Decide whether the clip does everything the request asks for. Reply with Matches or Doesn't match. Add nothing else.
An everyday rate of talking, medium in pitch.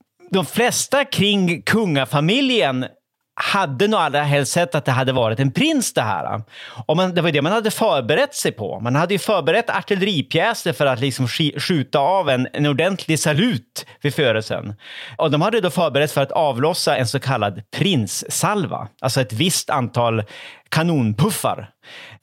Matches